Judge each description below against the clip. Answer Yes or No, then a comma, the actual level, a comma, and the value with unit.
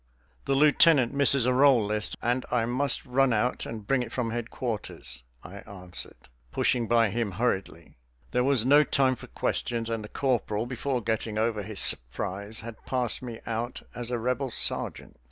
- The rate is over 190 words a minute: No, average, 170 wpm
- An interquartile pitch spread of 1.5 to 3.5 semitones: Yes, average, 2.8 semitones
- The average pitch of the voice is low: Yes, low, 120 Hz